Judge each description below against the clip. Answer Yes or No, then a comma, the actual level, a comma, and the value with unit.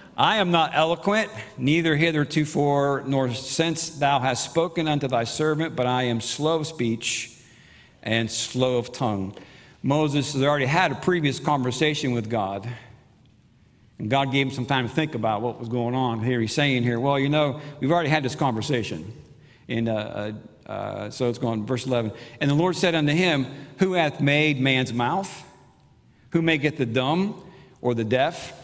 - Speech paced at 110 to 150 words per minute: No, average, 175 wpm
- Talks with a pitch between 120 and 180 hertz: Yes, low, 135 Hz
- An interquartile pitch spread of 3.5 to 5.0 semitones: Yes, average, 4.2 semitones